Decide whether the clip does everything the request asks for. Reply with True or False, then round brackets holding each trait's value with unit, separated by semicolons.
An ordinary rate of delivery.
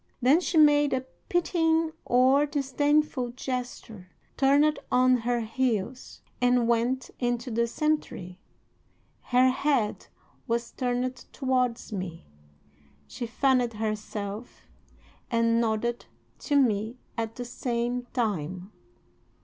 False (105 wpm)